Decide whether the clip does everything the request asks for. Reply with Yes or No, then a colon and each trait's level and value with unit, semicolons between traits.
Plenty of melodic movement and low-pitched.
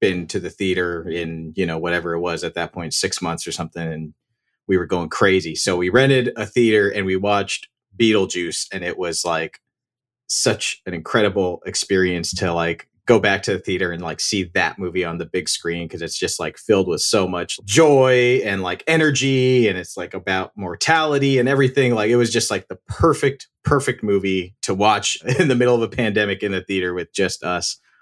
Yes: wide, 6.0 semitones; low, 100 Hz